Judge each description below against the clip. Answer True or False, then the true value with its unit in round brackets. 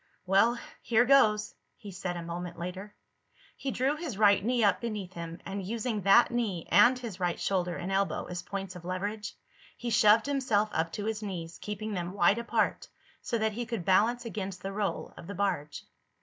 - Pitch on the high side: True (200 Hz)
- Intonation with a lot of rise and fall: False (3.9 semitones)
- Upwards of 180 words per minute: True (190 wpm)